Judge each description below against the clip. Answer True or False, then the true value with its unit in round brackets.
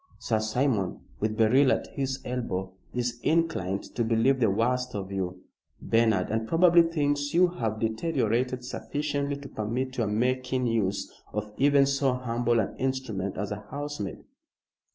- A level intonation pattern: False (4.1 semitones)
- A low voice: True (125 Hz)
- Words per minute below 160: True (150 wpm)